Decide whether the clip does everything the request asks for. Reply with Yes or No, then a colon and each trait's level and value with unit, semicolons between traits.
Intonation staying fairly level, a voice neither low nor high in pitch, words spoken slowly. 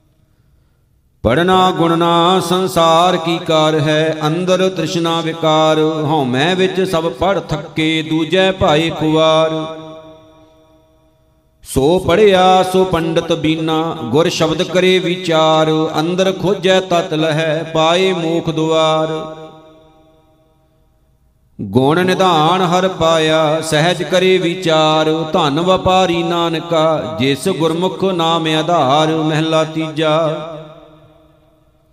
Yes: narrow, 1.7 semitones; medium, 160 Hz; slow, 90 wpm